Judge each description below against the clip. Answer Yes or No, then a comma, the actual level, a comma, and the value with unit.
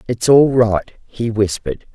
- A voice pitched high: No, low, 110 Hz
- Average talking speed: Yes, average, 155 wpm